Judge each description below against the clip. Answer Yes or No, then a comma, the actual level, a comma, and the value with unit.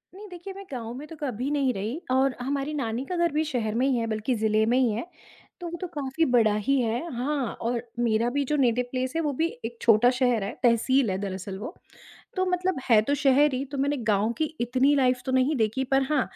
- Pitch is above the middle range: Yes, very high, 255 Hz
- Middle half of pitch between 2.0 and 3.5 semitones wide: No, average, 3.9 semitones